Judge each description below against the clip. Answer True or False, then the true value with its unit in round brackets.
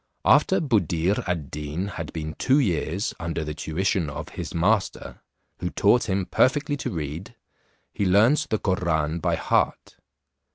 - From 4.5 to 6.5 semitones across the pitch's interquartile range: True (5.2 semitones)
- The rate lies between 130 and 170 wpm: True (150 wpm)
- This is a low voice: True (90 Hz)